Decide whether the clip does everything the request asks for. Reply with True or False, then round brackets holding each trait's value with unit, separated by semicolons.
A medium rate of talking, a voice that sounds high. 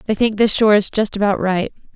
False (245 wpm; 205 Hz)